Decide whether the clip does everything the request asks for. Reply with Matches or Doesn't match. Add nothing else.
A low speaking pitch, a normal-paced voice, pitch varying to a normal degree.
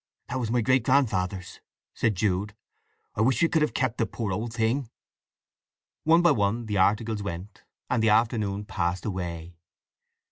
Matches